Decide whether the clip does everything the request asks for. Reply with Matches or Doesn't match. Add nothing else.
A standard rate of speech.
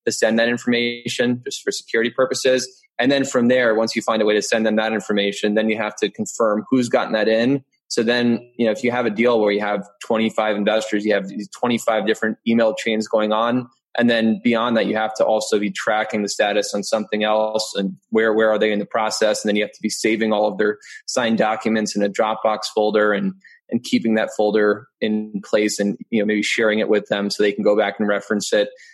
Doesn't match